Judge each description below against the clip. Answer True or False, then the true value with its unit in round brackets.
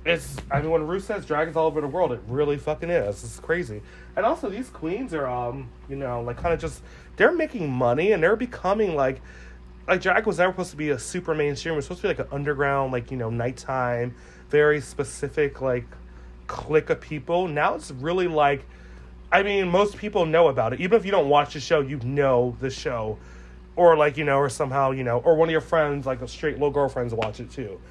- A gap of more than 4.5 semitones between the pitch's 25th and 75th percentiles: True (5.0 semitones)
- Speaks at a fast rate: True (230 wpm)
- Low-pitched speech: False (145 Hz)